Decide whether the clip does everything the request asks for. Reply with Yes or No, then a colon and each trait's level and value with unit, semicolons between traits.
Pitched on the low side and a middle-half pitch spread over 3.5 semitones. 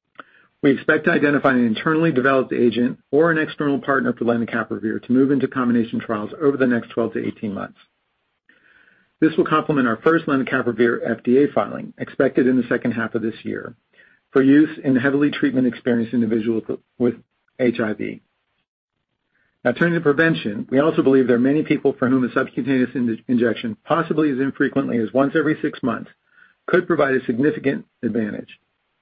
No: low, 130 Hz; average, 3.2 semitones